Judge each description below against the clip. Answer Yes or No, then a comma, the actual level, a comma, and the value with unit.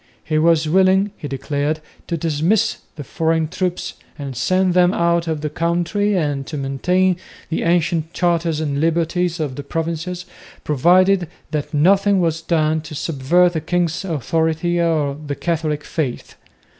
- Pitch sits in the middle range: Yes, medium, 165 Hz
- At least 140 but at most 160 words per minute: Yes, average, 150 wpm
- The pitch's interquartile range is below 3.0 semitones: Yes, narrow, 2.6 semitones